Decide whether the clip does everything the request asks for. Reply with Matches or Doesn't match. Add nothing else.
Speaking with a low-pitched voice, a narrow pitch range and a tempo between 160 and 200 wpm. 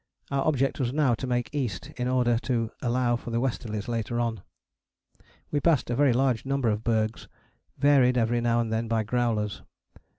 Matches